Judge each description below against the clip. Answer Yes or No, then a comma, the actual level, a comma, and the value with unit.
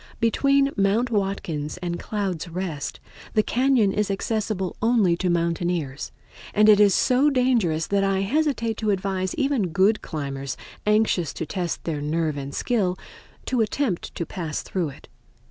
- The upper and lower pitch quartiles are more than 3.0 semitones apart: Yes, average, 4.7 semitones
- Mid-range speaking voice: No, high, 195 Hz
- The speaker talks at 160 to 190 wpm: No, average, 150 wpm